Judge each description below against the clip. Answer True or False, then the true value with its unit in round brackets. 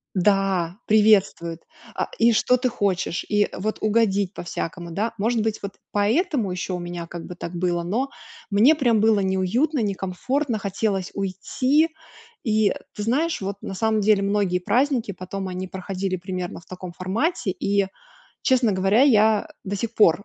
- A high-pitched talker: True (200 Hz)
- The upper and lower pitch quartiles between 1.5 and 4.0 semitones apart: True (3.3 semitones)